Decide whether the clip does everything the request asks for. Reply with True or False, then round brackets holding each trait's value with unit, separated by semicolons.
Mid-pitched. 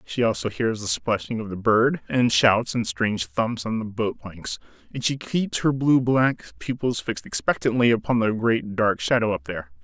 False (115 Hz)